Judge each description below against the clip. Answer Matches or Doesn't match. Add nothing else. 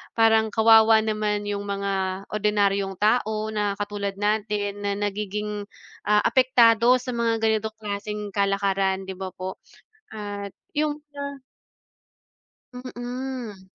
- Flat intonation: Matches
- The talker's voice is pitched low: Doesn't match